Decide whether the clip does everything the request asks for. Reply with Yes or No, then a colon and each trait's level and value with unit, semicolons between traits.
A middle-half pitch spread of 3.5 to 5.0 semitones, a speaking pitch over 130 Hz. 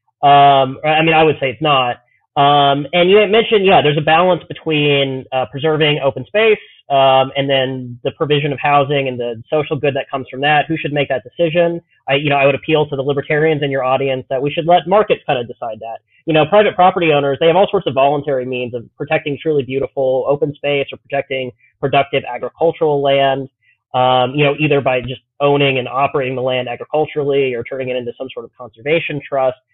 No: average, 2.9 semitones; medium, 140 Hz